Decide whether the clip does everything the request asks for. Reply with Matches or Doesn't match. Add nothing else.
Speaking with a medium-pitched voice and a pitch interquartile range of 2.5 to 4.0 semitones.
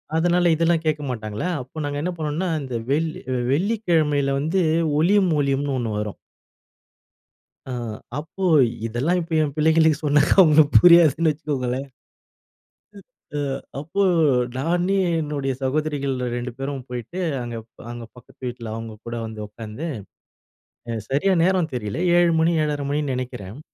Doesn't match